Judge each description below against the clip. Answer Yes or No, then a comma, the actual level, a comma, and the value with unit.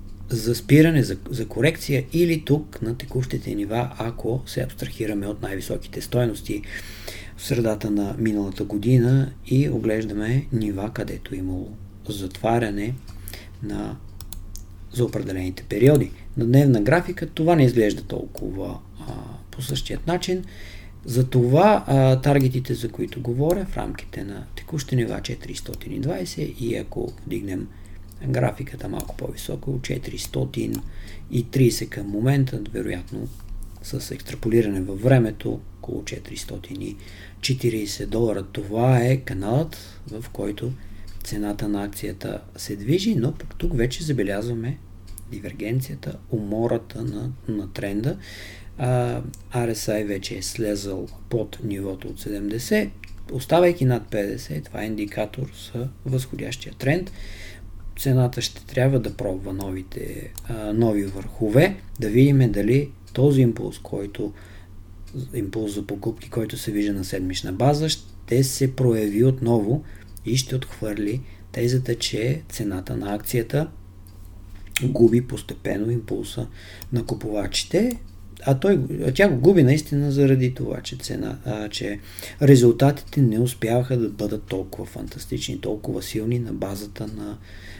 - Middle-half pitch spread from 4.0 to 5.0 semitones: Yes, average, 4.6 semitones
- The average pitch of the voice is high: No, low, 110 Hz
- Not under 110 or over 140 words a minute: Yes, average, 120 wpm